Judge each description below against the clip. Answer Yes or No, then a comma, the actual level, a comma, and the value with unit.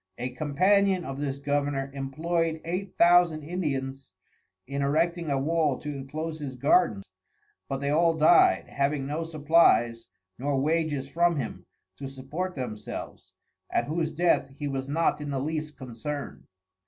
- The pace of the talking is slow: No, average, 145 wpm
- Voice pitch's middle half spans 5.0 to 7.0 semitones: No, average, 3.3 semitones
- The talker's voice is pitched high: No, medium, 145 Hz